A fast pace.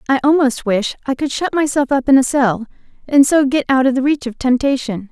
Yes: fast, 235 wpm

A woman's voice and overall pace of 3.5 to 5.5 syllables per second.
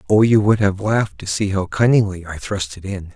No: male; 5.4 syllables/s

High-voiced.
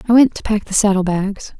Yes: high, 205 Hz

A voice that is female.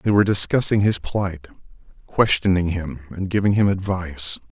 No: male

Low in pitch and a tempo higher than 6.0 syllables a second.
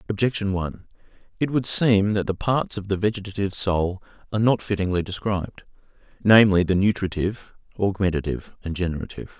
Yes: low, 100 Hz; 6.3 syllables/s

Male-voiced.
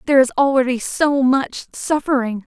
No: female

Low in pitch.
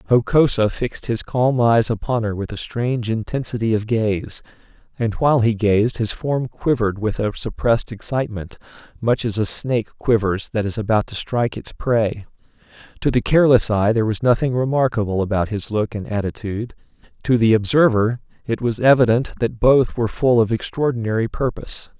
Yes: low, 115 Hz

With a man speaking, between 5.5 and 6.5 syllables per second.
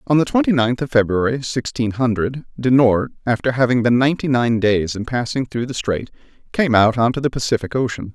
Yes: male; 5.6 syllables/s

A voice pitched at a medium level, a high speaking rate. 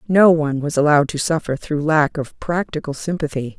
No: medium, 155 Hz; average, 185 wpm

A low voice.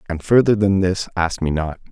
Yes: very low, 95 Hz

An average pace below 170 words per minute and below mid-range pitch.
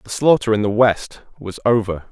No: average, 200 wpm; low, 110 Hz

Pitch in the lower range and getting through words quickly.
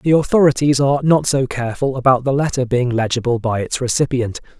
No: low, 130 Hz; average, 185 wpm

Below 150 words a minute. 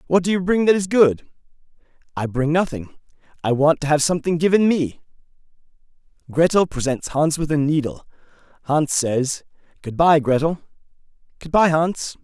Yes: average, 140 wpm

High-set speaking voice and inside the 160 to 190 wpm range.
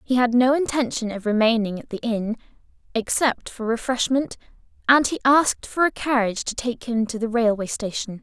Yes: high, 235 Hz; average, 180 wpm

